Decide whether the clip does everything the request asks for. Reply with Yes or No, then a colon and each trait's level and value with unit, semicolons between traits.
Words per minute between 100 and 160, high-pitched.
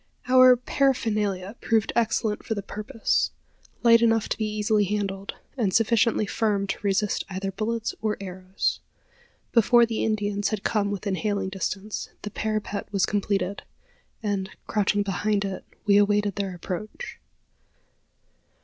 Yes: slow, 135 wpm; high, 210 Hz